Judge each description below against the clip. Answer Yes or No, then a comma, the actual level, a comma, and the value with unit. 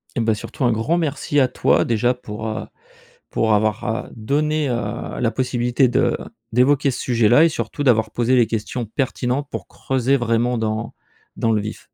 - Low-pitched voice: Yes, low, 120 Hz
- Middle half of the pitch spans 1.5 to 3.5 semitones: Yes, average, 3.0 semitones